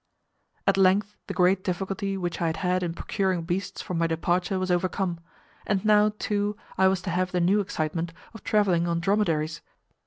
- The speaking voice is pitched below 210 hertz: Yes, medium, 185 Hz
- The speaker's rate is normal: Yes, average, 185 wpm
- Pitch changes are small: Yes, narrow, 2.3 semitones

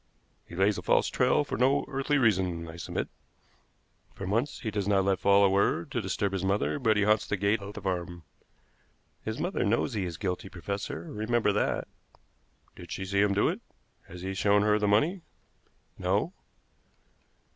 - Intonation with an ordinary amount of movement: No, narrow, 2.3 semitones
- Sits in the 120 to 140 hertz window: No, low, 100 Hz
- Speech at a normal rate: Yes, average, 185 wpm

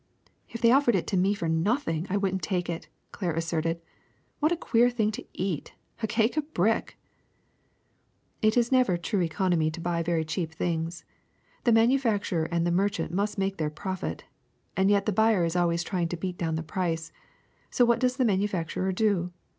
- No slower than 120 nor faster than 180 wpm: No, average, 200 wpm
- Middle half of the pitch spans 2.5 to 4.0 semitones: No, average, 4.5 semitones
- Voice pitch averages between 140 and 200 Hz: Yes, high, 190 Hz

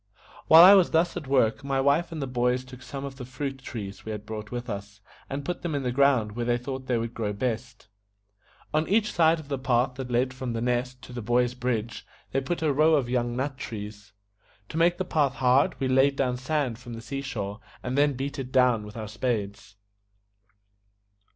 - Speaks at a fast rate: Yes, fast, 220 wpm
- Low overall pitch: Yes, low, 130 Hz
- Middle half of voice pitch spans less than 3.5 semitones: Yes, average, 2.9 semitones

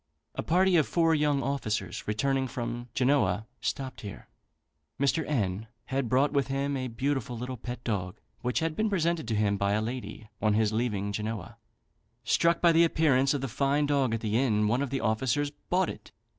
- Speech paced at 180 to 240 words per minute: Yes, average, 190 wpm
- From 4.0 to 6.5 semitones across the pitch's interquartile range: Yes, average, 4.6 semitones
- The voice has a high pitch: No, low, 130 Hz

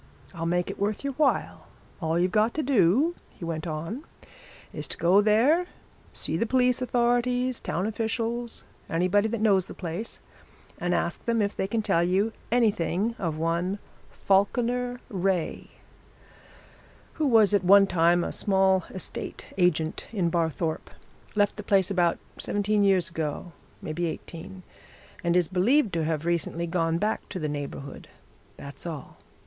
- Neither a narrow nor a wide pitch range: Yes, average, 4.9 semitones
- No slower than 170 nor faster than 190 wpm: No, average, 155 wpm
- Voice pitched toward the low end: No, high, 190 Hz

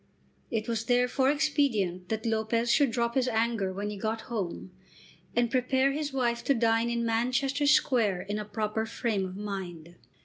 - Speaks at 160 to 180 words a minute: Yes, average, 170 wpm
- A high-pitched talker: Yes, high, 230 Hz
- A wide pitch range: No, average, 3.1 semitones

